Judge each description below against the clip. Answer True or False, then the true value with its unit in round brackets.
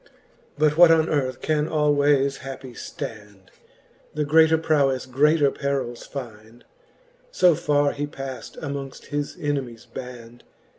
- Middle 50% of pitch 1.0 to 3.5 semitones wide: True (2.7 semitones)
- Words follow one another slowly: True (120 wpm)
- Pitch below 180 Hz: True (140 Hz)